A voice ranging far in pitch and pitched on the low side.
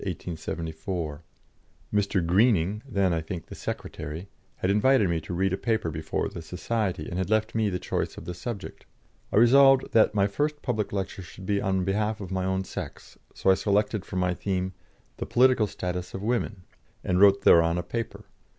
No: average, 3.3 semitones; very low, 95 Hz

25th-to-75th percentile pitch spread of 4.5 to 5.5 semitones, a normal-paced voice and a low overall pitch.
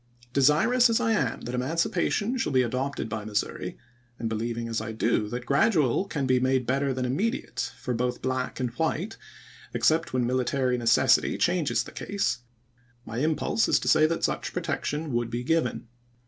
Yes: average, 5.0 semitones; average, 175 wpm; low, 130 Hz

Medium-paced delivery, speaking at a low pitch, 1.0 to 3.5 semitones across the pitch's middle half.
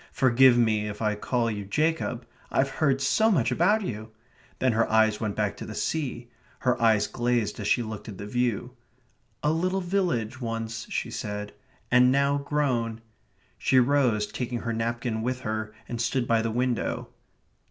Yes: average, 175 wpm; low, 120 Hz; average, 3.2 semitones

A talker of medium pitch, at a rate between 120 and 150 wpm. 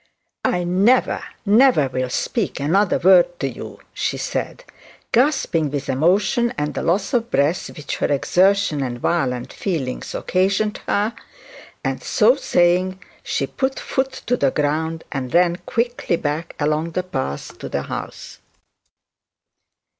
Yes: medium, 175 Hz; average, 140 wpm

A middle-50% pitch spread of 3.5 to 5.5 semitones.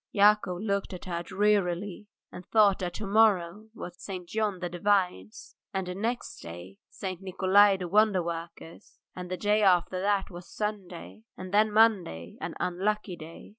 No: average, 2.9 semitones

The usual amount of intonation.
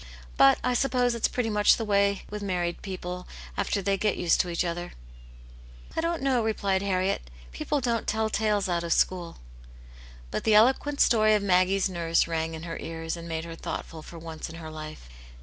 Yes: average, 4.5 semitones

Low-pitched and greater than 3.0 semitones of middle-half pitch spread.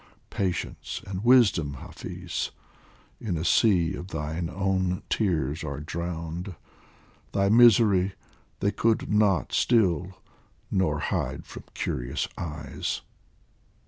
Yes: very low, 90 Hz; average, 3.6 semitones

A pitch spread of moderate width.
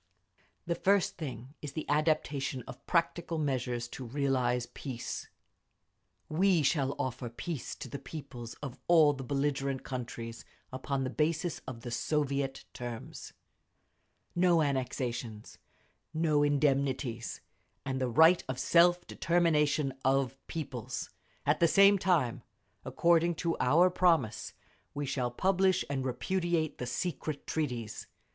Yes: average, 4.4 semitones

